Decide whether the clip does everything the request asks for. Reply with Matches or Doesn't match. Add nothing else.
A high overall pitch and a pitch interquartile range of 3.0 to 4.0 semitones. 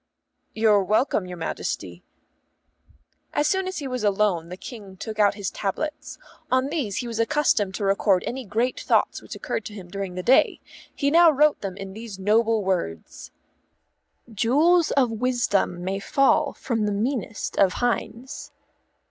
Doesn't match